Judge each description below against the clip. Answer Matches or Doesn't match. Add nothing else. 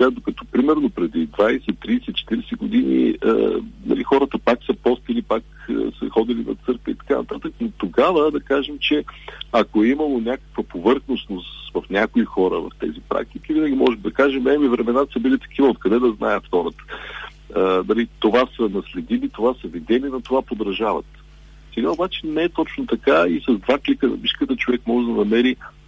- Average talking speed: Doesn't match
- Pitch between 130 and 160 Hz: Matches